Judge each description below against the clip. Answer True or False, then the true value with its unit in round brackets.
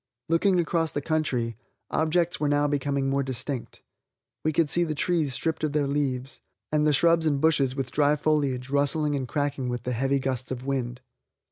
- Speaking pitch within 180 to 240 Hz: False (145 Hz)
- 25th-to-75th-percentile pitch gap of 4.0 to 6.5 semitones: False (2.8 semitones)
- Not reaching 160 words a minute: False (190 wpm)